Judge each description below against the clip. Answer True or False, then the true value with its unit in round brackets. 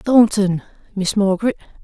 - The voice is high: True (205 Hz)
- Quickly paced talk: False (100 wpm)